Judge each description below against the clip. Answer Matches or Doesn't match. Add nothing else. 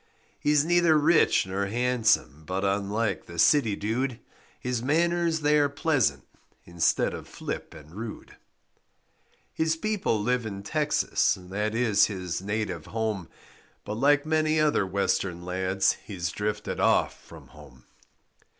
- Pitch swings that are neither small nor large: Doesn't match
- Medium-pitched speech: Doesn't match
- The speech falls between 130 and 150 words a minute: Matches